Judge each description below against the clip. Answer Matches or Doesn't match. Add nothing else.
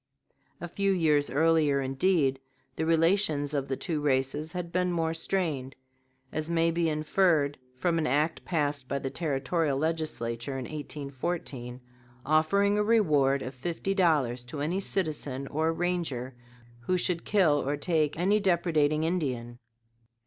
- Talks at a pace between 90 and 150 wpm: Matches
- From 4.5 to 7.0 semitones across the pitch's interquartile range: Doesn't match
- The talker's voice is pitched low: Doesn't match